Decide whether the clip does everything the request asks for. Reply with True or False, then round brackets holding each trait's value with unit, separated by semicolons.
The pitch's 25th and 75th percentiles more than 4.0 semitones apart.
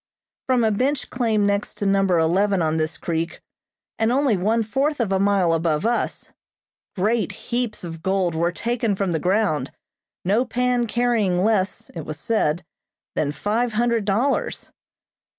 True (4.9 semitones)